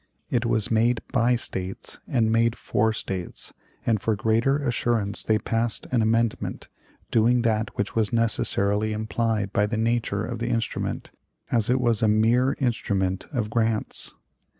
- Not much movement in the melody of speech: Yes, narrow, 1.8 semitones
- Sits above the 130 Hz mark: No, low, 115 Hz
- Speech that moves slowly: No, average, 150 wpm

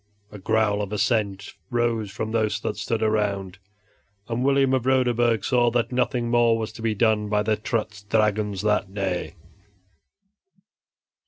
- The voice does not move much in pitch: Yes, narrow, 2.3 semitones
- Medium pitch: No, low, 110 Hz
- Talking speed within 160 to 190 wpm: No, average, 150 wpm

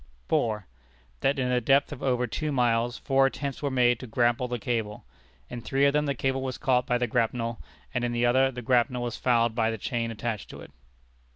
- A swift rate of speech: Yes, fast, 220 wpm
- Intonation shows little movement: Yes, narrow, 2.2 semitones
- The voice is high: No, low, 125 Hz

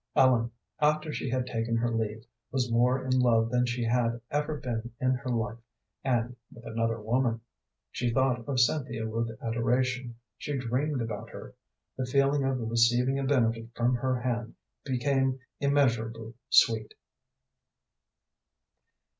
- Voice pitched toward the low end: Yes, low, 120 Hz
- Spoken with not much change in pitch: Yes, narrow, 2.2 semitones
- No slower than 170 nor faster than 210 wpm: No, average, 140 wpm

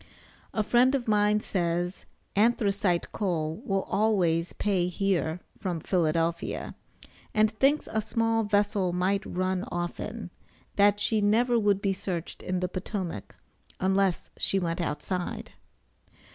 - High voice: Yes, high, 195 Hz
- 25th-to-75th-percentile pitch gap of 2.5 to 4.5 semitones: Yes, average, 3.0 semitones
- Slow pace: Yes, slow, 125 wpm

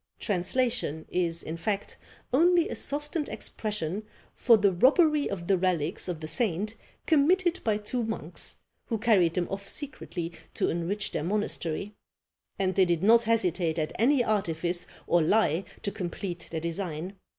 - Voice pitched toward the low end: No, high, 195 Hz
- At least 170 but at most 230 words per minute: No, average, 150 wpm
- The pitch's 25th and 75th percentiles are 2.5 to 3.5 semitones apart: No, average, 5.2 semitones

